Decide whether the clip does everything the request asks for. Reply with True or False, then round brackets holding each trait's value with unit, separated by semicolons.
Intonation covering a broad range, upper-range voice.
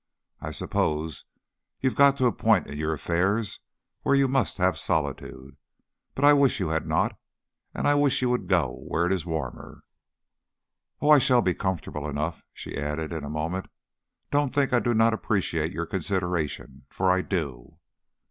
False (7.9 semitones; 90 Hz)